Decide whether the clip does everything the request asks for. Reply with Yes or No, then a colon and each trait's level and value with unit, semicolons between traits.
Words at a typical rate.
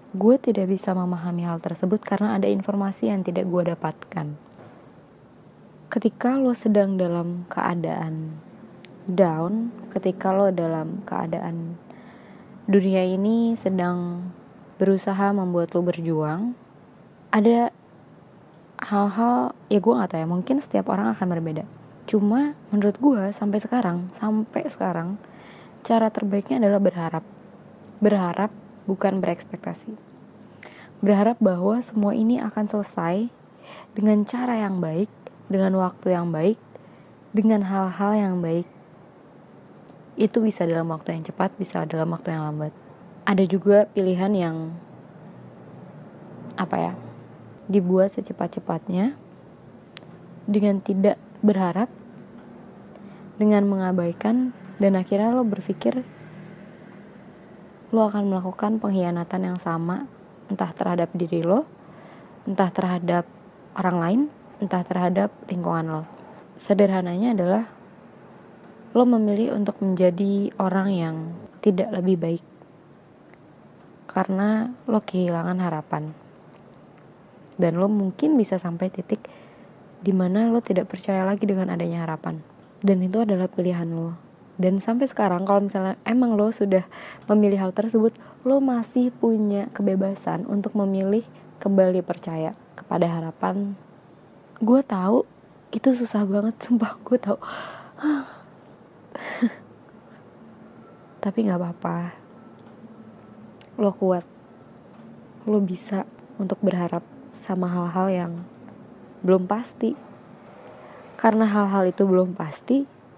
Yes: average, 105 wpm